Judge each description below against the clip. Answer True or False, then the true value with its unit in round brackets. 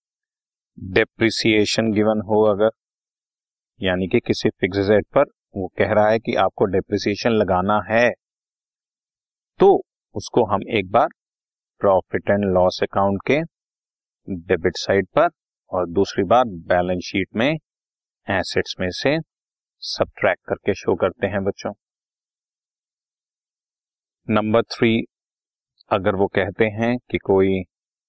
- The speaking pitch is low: True (105 Hz)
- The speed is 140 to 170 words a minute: False (115 wpm)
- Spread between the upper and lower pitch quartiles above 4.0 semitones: False (2.7 semitones)